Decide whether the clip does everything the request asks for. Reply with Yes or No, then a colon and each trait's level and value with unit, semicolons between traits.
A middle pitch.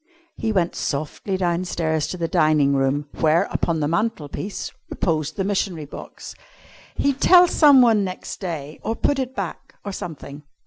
Yes: medium, 170 Hz